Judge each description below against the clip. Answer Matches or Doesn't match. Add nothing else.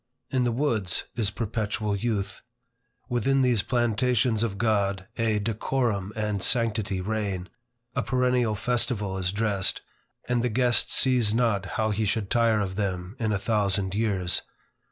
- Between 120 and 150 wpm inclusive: Matches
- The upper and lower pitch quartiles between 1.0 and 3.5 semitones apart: Matches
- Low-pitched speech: Matches